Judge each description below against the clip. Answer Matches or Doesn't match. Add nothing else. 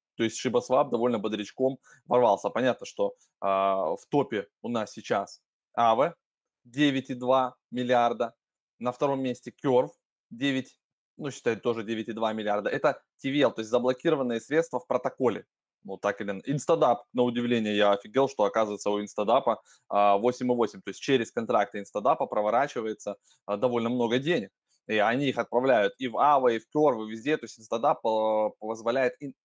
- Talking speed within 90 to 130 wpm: Doesn't match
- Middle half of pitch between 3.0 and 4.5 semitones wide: Matches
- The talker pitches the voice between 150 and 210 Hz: Doesn't match